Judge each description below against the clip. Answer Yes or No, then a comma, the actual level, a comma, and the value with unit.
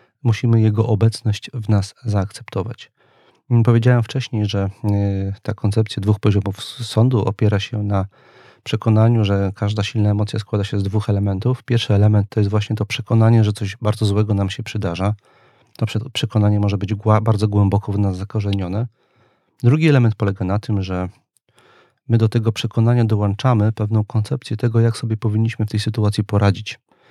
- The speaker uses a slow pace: No, average, 155 wpm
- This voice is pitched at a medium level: No, low, 110 Hz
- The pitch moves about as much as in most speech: No, narrow, 2.1 semitones